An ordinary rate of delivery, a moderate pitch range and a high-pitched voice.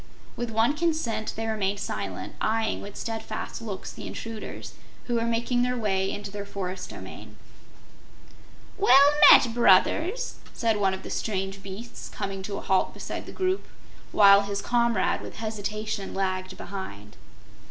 Yes: average, 150 wpm; average, 3.2 semitones; high, 215 Hz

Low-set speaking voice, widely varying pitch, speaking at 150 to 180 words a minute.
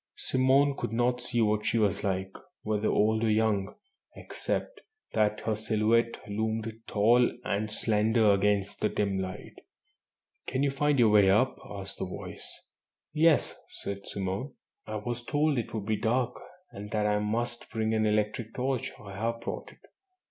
No: low, 110 Hz; narrow, 2.5 semitones; average, 165 wpm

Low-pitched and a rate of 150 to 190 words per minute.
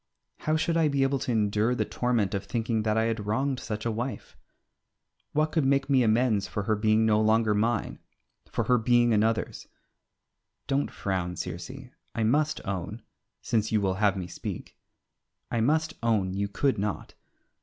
Yes: low, 110 Hz; average, 175 wpm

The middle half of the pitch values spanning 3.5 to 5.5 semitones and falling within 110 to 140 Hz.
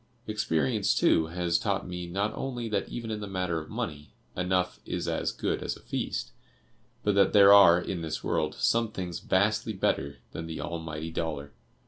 No: average, 3.8 semitones; very low, 90 Hz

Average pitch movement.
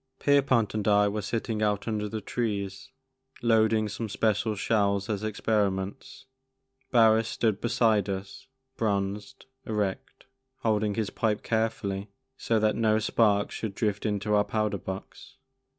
No: narrow, 1.7 semitones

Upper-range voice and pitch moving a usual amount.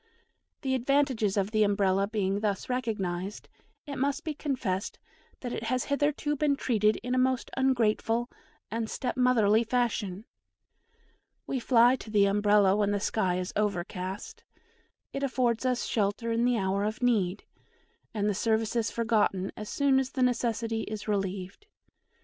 Yes: high, 225 Hz; average, 3.8 semitones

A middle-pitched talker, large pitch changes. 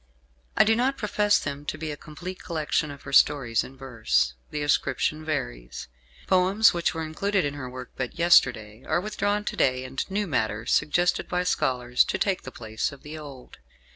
Yes: medium, 150 Hz; wide, 5.9 semitones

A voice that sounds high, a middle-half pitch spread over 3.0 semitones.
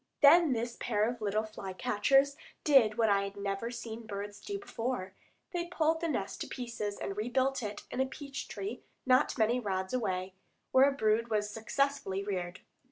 Yes: high, 230 Hz; average, 4.7 semitones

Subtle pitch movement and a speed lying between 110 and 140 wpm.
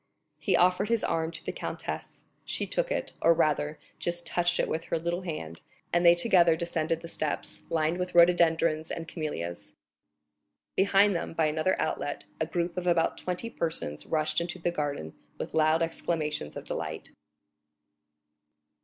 No: narrow, 1.9 semitones; average, 160 wpm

